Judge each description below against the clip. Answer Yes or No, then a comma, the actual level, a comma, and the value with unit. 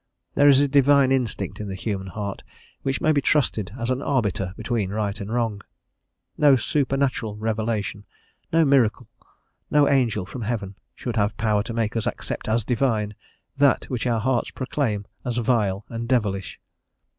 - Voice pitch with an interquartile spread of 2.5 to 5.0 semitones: Yes, average, 4.1 semitones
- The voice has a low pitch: Yes, low, 115 Hz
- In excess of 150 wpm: Yes, average, 165 wpm